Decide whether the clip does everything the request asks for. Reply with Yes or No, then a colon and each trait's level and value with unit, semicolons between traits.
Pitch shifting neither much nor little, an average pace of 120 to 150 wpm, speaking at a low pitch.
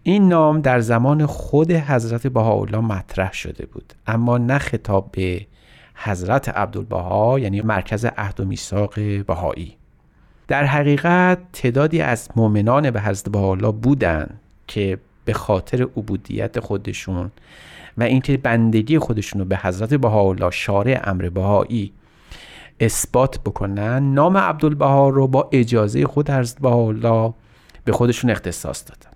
Yes: average, 4.9 semitones; average, 125 wpm; low, 115 Hz